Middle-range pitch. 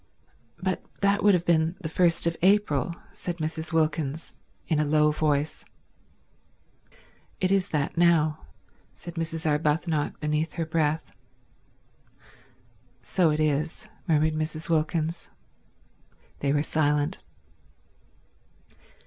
Yes: medium, 160 Hz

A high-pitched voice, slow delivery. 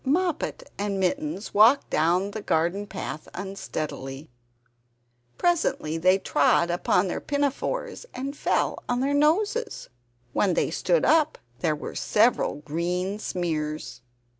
Yes: high, 200 Hz; slow, 120 wpm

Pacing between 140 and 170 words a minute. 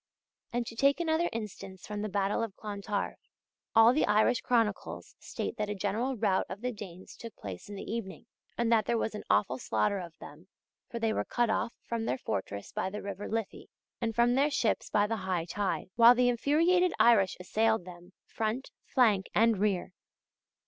No: average, 190 wpm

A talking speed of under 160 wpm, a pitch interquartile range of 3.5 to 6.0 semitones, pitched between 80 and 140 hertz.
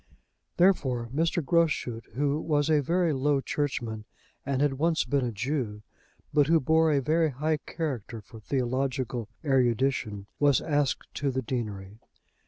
Yes: average, 145 wpm; average, 4.0 semitones; low, 135 Hz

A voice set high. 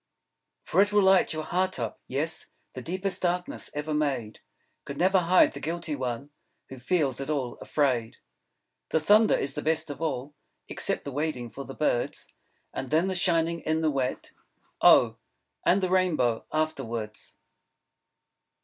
No: medium, 155 Hz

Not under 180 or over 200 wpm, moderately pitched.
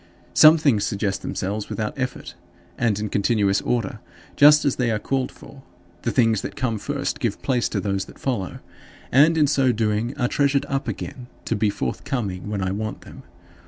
No: average, 185 wpm; low, 120 Hz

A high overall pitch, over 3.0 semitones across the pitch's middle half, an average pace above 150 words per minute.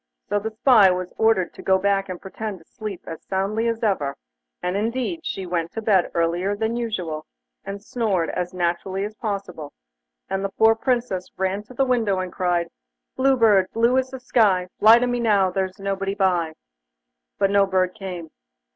Yes: high, 195 Hz; average, 3.4 semitones; average, 185 wpm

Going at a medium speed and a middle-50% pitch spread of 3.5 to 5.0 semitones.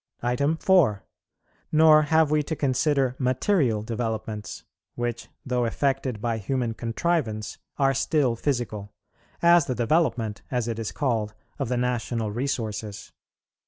No: slow, 125 wpm; average, 4.1 semitones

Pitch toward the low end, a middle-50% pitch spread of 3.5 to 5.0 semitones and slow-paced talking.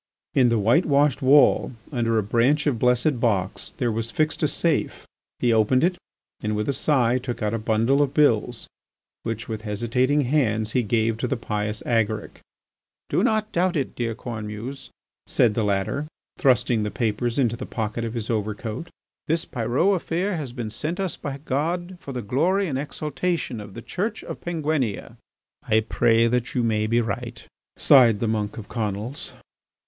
No: low, 120 Hz; average, 4.6 semitones; average, 175 wpm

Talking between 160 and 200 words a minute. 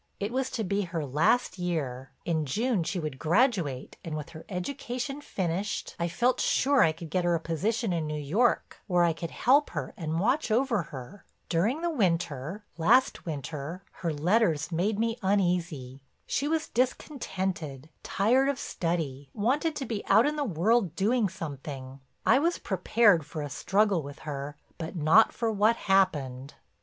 Yes: average, 165 wpm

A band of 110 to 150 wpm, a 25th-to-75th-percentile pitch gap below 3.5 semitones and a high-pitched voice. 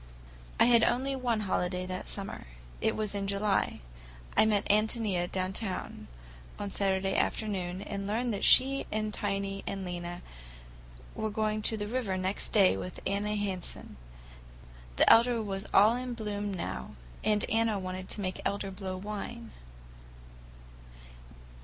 Yes: average, 140 wpm; narrow, 2.6 semitones; high, 200 Hz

